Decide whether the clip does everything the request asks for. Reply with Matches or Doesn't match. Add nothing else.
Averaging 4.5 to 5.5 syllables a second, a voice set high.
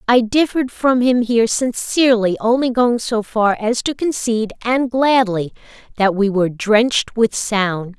Matches